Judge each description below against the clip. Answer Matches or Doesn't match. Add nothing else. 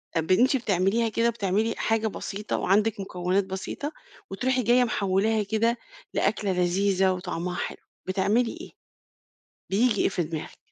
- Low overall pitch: Doesn't match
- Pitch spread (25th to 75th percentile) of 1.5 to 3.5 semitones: Matches